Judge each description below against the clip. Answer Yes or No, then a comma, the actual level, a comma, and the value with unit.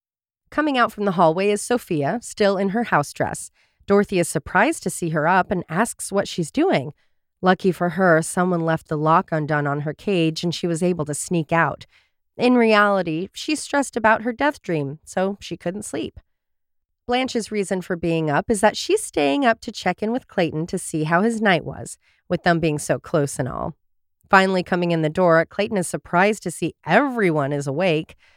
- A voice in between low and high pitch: Yes, medium, 180 Hz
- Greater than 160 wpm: Yes, average, 200 wpm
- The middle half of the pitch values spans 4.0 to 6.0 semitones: Yes, average, 4.4 semitones